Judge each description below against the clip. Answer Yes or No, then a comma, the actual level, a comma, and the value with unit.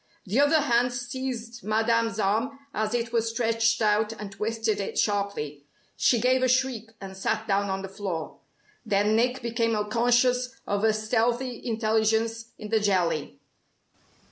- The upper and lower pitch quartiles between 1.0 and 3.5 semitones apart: Yes, narrow, 2.5 semitones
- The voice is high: Yes, high, 225 Hz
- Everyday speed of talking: Yes, average, 150 wpm